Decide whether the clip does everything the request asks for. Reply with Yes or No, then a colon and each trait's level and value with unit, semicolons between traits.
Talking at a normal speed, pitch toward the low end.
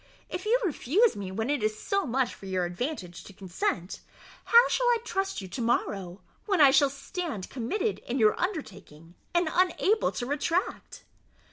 No: average, 170 wpm; very high, 270 Hz